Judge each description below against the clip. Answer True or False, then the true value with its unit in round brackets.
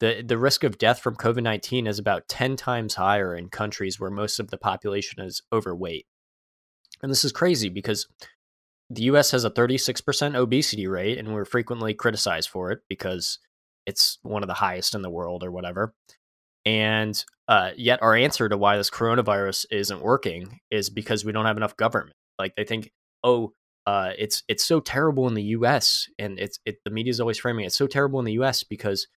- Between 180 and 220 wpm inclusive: True (205 wpm)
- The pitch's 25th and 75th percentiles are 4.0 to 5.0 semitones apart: False (3.2 semitones)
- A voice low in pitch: True (110 Hz)